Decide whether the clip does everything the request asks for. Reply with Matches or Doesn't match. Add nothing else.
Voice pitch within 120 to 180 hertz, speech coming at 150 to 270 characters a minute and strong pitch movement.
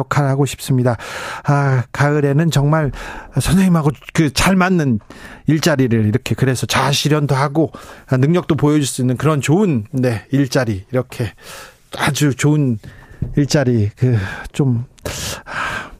Doesn't match